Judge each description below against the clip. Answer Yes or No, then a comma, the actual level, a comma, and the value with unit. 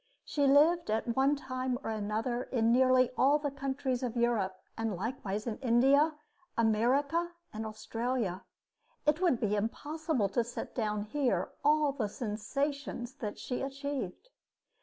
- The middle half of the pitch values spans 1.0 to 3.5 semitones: No, average, 4.3 semitones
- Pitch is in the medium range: No, very high, 250 Hz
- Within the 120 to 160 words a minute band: Yes, average, 140 wpm